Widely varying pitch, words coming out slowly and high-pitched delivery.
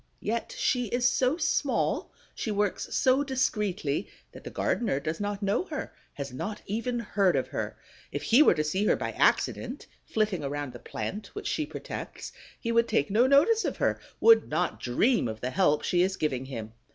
No: wide, 8.6 semitones; average, 190 wpm; high, 210 Hz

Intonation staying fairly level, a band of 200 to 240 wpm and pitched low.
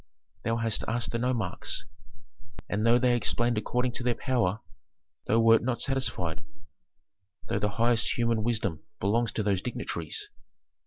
No: narrow, 2.1 semitones; average, 145 wpm; low, 115 Hz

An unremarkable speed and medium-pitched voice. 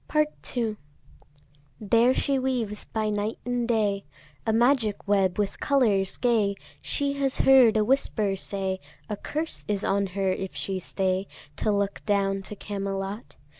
No: average, 150 wpm; high, 210 Hz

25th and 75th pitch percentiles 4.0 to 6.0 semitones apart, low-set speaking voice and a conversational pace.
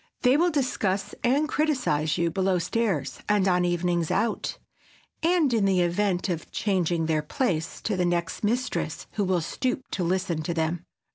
No: wide, 5.4 semitones; medium, 185 Hz; average, 165 wpm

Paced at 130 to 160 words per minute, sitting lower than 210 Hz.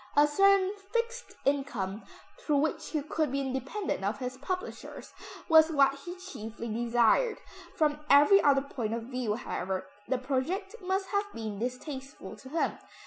No: average, 150 wpm; very high, 280 Hz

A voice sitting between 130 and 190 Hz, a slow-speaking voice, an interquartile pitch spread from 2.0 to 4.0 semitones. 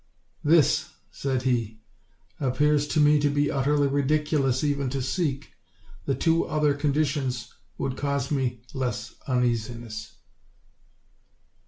Yes: medium, 140 Hz; slow, 120 wpm; average, 2.7 semitones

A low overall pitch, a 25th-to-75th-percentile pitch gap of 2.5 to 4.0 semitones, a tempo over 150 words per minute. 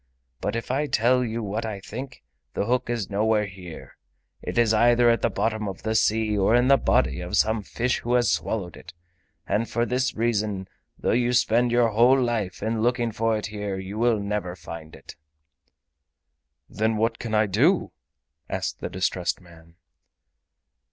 Yes: low, 110 Hz; average, 2.9 semitones; average, 175 wpm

